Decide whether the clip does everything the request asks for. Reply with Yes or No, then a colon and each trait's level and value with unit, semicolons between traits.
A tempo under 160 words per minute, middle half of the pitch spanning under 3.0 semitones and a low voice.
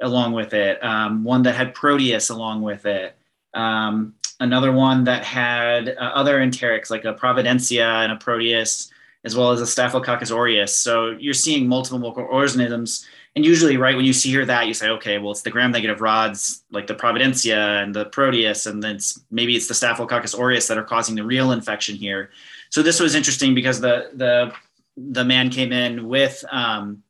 No: average, 190 wpm; narrow, 2.6 semitones; low, 120 Hz